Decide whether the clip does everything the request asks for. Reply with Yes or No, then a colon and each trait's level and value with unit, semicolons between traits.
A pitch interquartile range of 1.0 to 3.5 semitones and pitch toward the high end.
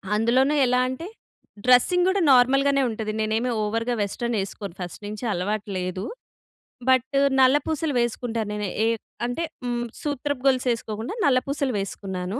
No: average, 4.0 semitones; high, 245 Hz